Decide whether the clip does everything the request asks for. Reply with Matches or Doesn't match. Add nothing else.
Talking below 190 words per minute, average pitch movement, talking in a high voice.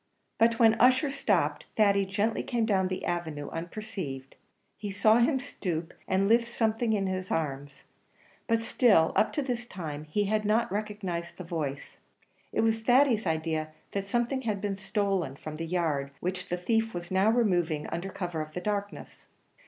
Matches